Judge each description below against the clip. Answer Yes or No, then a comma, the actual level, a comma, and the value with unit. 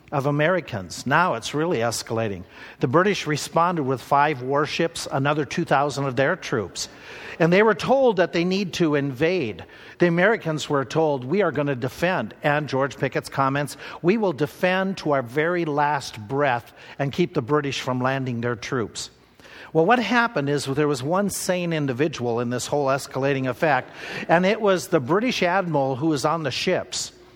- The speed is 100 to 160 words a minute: No, average, 175 wpm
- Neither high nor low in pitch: Yes, medium, 150 Hz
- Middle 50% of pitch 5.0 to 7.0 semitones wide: No, average, 4.2 semitones